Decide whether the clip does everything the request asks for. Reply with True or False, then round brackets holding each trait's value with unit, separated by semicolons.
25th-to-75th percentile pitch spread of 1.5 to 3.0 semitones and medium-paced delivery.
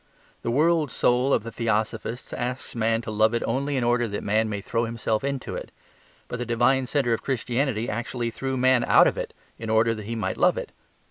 False (2.5 semitones; 215 wpm)